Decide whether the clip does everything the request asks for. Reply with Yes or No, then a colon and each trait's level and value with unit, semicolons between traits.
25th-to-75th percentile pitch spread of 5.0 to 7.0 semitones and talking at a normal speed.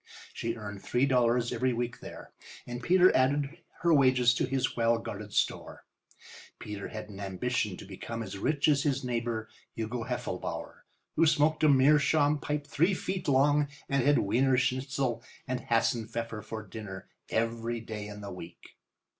No: average, 3.8 semitones; average, 160 wpm